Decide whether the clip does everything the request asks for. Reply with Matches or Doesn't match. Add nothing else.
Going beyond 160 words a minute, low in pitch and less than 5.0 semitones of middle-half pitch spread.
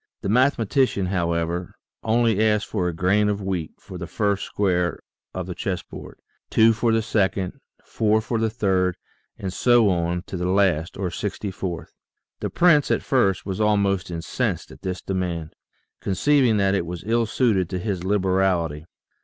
Matches